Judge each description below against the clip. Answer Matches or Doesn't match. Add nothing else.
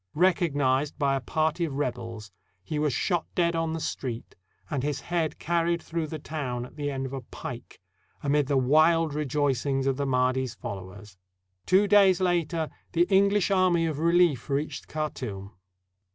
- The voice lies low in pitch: Doesn't match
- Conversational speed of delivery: Matches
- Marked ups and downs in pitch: Doesn't match